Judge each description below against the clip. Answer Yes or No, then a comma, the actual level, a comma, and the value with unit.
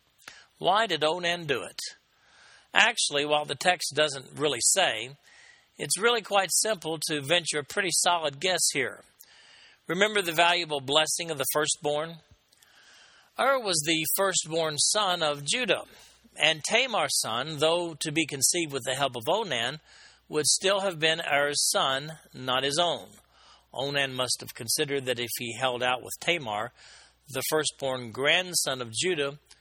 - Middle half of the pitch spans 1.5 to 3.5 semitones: No, average, 4.1 semitones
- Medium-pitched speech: Yes, medium, 155 Hz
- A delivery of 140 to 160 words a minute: Yes, average, 150 wpm